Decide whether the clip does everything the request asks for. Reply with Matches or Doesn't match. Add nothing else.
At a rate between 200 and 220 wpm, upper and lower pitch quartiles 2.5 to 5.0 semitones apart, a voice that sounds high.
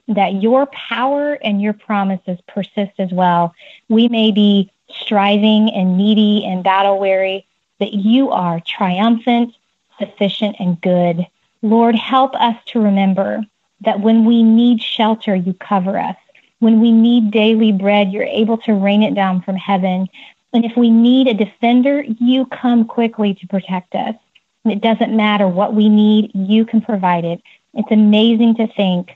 Doesn't match